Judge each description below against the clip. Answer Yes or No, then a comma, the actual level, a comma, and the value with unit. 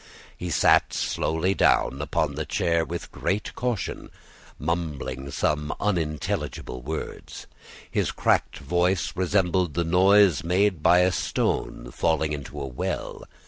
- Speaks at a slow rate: Yes, slow, 125 wpm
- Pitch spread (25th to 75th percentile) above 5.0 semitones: No, average, 3.5 semitones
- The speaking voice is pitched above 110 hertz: No, very low, 85 Hz